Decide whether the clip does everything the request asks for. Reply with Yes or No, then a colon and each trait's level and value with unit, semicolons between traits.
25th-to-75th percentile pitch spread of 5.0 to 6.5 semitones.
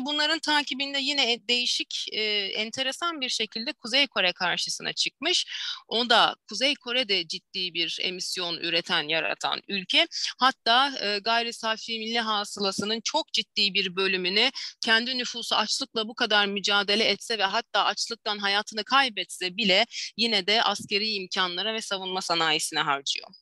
No: average, 4.2 semitones